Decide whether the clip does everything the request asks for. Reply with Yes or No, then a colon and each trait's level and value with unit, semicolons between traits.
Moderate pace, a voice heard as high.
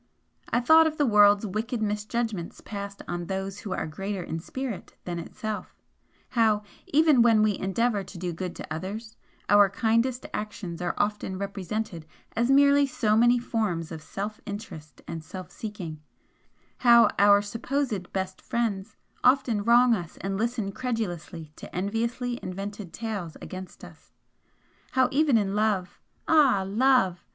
Yes: average, 145 wpm; high, 210 Hz